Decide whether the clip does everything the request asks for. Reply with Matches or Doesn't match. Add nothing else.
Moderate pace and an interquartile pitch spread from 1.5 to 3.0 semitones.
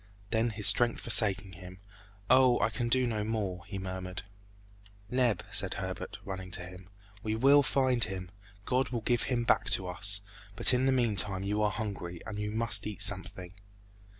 Doesn't match